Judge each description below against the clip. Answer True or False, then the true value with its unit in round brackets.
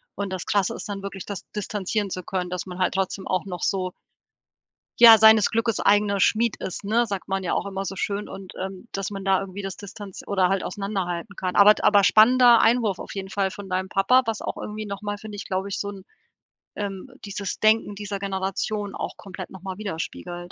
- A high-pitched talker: True (195 Hz)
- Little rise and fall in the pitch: True (1.7 semitones)